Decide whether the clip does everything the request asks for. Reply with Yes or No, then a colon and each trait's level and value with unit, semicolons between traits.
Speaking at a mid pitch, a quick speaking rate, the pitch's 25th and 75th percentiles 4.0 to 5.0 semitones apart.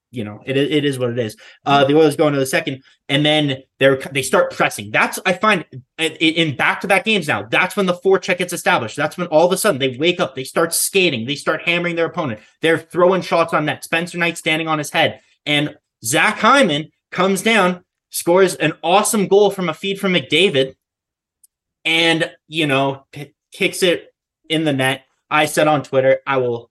Yes: medium, 160 Hz; fast, 215 wpm; average, 4.7 semitones